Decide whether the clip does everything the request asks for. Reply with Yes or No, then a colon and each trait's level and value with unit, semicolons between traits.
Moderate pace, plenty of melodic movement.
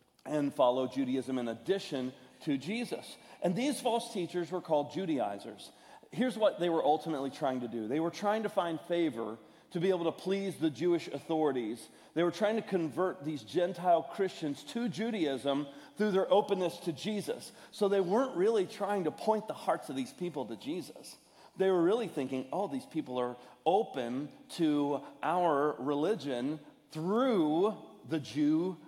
Yes: average, 165 wpm; wide, 5.7 semitones